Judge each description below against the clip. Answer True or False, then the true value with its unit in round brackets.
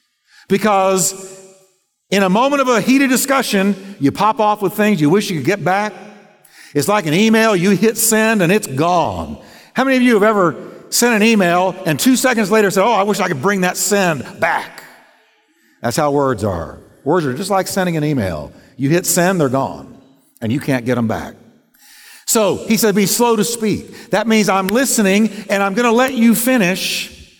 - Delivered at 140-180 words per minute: False (200 wpm)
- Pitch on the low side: False (195 Hz)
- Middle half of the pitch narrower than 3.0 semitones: False (3.7 semitones)